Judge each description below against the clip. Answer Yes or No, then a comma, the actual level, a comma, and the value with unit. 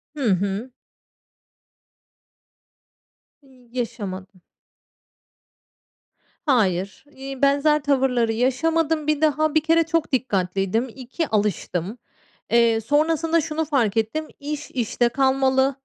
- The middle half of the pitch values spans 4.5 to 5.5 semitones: Yes, average, 5.2 semitones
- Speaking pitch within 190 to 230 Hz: No, very high, 265 Hz